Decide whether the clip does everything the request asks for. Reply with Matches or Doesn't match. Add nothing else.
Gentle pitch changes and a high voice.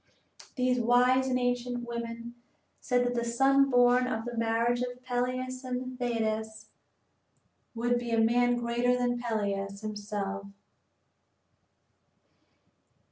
Matches